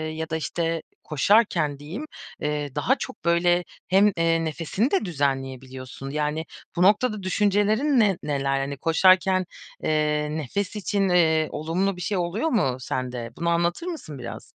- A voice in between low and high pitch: Yes, medium, 165 Hz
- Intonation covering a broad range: No, average, 4.9 semitones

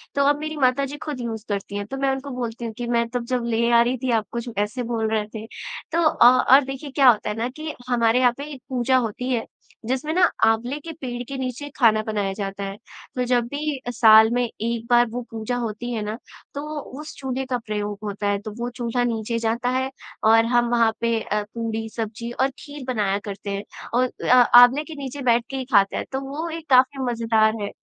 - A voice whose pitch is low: No, high, 240 Hz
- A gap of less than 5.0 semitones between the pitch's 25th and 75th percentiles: Yes, average, 2.9 semitones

